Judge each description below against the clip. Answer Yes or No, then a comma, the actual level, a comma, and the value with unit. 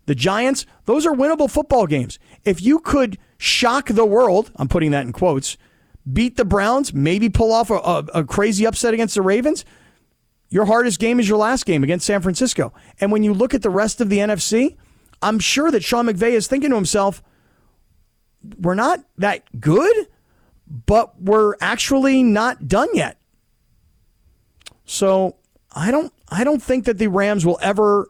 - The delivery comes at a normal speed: Yes, average, 175 wpm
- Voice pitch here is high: Yes, high, 215 Hz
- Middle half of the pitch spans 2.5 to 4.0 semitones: No, average, 4.7 semitones